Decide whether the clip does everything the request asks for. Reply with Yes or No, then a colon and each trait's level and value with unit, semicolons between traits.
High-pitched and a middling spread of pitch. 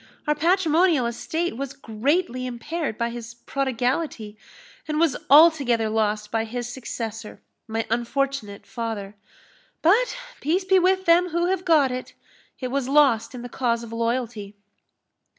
No: very high, 255 Hz; wide, 5.7 semitones